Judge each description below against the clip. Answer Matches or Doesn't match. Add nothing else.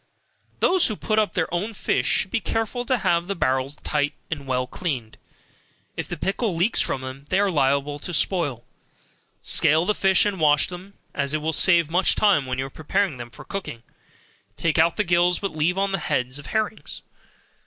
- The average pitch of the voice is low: Doesn't match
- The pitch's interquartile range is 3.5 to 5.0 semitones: Doesn't match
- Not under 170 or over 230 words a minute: Matches